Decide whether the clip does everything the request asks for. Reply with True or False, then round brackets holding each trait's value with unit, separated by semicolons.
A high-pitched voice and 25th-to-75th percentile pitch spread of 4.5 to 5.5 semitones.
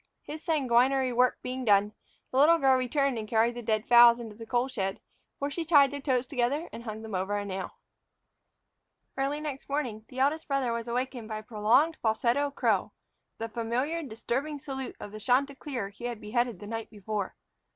False (245 Hz; 3.9 semitones)